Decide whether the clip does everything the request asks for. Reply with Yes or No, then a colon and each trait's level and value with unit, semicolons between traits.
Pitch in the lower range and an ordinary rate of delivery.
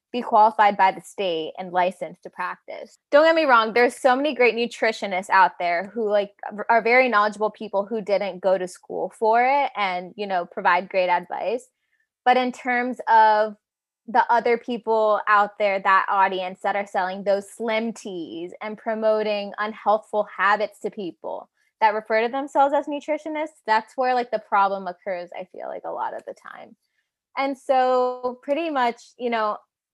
No: high, 220 Hz; average, 175 wpm